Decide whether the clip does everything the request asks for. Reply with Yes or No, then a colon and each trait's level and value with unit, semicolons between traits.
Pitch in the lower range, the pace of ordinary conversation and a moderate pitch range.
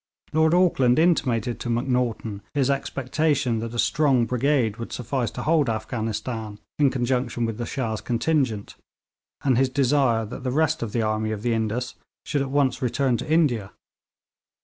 Yes: low, 125 Hz; average, 165 wpm; average, 3.5 semitones